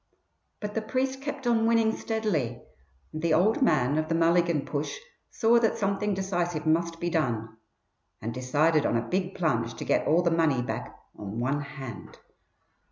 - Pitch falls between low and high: Yes, medium, 165 Hz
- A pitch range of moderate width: No, wide, 6.8 semitones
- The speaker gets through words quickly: No, average, 170 wpm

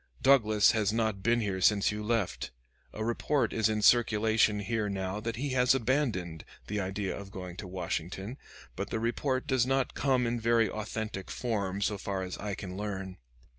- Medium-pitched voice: No, low, 105 Hz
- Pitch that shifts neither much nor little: Yes, average, 3.3 semitones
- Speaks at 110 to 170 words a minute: No, average, 180 wpm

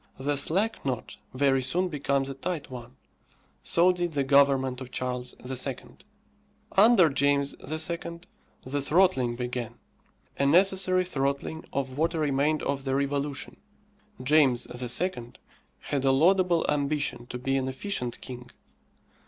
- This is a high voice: No, medium, 140 Hz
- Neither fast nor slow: No, slow, 130 wpm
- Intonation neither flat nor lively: Yes, average, 4.0 semitones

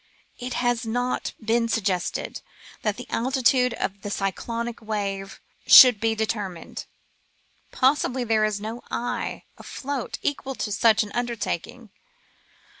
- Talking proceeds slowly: Yes, slow, 125 wpm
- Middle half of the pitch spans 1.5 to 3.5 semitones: Yes, average, 2.8 semitones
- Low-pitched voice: No, high, 230 Hz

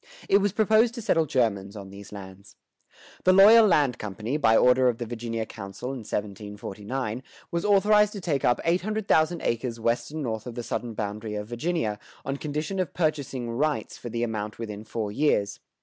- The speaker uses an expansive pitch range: Yes, wide, 7.2 semitones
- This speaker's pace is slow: No, average, 185 wpm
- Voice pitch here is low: Yes, low, 120 Hz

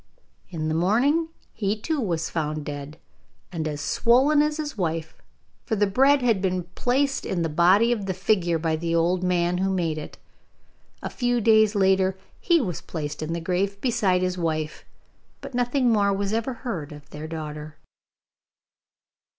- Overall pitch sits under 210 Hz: Yes, medium, 185 Hz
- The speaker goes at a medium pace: Yes, average, 170 wpm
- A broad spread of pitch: Yes, wide, 6.0 semitones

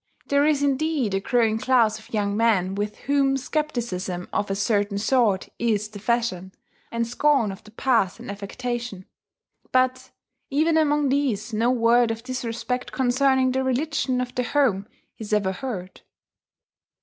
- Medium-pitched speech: No, high, 235 Hz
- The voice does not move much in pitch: No, average, 4.2 semitones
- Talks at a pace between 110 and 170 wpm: Yes, average, 150 wpm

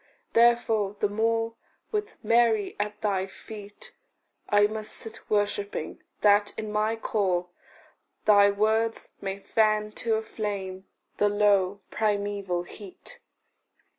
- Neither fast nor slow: No, slow, 115 wpm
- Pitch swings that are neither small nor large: No, narrow, 1.5 semitones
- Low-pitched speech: No, high, 210 Hz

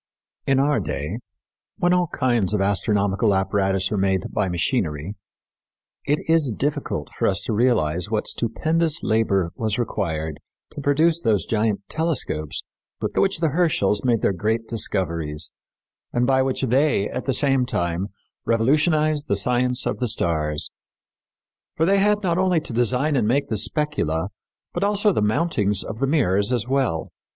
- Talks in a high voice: No, low, 115 Hz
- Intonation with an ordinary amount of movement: No, wide, 7.0 semitones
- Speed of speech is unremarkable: Yes, average, 160 wpm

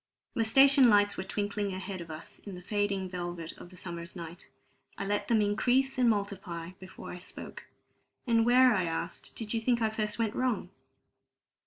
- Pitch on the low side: No, high, 205 Hz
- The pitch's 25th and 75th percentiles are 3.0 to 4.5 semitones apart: Yes, average, 3.9 semitones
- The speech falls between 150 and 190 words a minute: Yes, average, 185 wpm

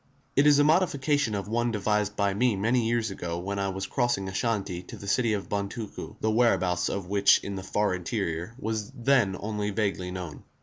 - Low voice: Yes, low, 105 Hz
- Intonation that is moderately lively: Yes, average, 3.3 semitones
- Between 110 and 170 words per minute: No, average, 200 wpm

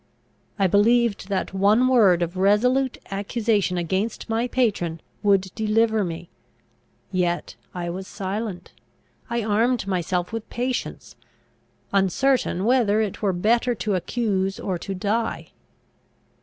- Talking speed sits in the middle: No, slow, 120 wpm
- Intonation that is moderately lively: Yes, average, 3.6 semitones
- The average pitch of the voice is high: Yes, high, 205 Hz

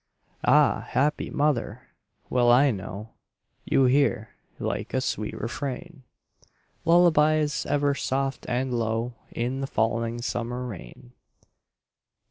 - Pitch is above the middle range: No, low, 125 Hz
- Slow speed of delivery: Yes, slow, 105 wpm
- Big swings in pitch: No, average, 3.5 semitones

